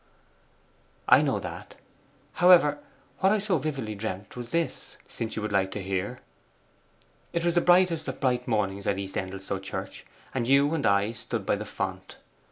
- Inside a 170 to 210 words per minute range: Yes, average, 175 wpm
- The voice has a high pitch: No, low, 120 Hz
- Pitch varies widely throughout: Yes, wide, 8.1 semitones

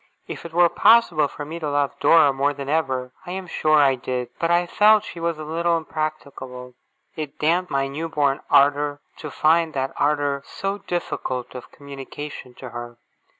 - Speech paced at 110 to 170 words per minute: No, average, 185 wpm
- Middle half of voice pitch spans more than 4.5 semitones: No, average, 3.3 semitones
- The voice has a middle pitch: Yes, medium, 150 Hz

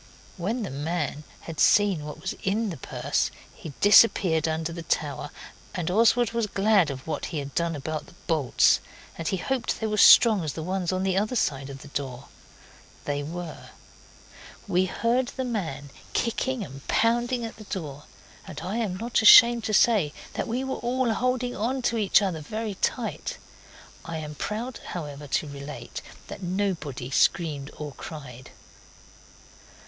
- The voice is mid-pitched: Yes, medium, 180 Hz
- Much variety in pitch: Yes, wide, 6.9 semitones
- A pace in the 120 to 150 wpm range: No, average, 170 wpm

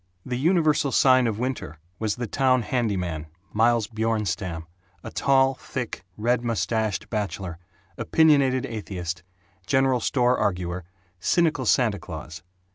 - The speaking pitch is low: Yes, low, 115 Hz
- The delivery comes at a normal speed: No, slow, 120 wpm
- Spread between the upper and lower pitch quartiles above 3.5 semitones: Yes, average, 5.0 semitones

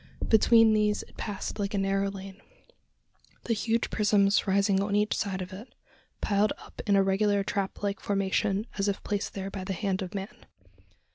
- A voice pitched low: No, high, 200 Hz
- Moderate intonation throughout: No, narrow, 1.2 semitones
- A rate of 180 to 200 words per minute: Yes, average, 185 wpm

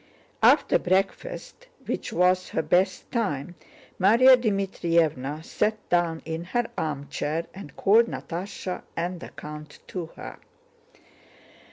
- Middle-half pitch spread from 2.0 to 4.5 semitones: Yes, average, 3.6 semitones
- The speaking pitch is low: No, medium, 180 Hz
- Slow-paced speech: Yes, slow, 115 wpm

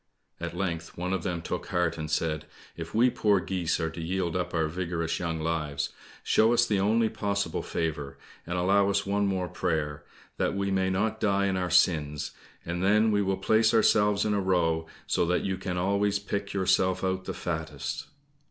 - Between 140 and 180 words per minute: No, average, 195 wpm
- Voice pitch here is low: Yes, very low, 95 Hz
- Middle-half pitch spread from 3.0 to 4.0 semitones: Yes, average, 3.3 semitones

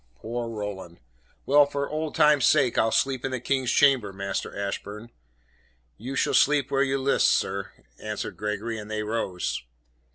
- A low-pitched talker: Yes, low, 115 Hz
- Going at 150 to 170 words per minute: Yes, average, 160 wpm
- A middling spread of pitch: Yes, average, 4.7 semitones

